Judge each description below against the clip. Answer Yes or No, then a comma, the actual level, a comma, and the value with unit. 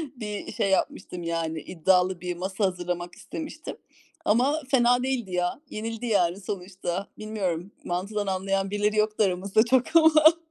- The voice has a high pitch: Yes, high, 200 Hz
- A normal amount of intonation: Yes, average, 4.0 semitones